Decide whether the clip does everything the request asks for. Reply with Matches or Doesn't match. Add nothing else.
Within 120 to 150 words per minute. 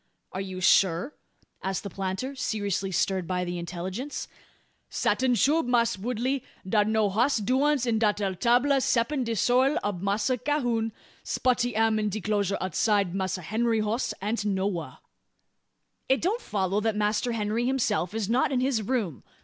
Doesn't match